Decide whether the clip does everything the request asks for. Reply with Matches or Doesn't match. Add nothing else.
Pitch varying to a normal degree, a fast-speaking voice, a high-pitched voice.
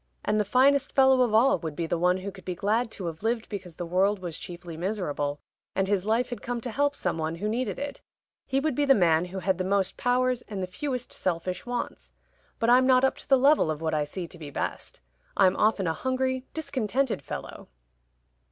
Doesn't match